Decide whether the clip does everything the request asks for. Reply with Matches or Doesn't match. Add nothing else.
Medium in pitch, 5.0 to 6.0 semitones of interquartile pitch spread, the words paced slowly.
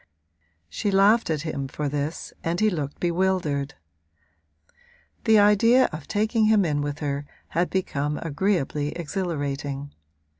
Matches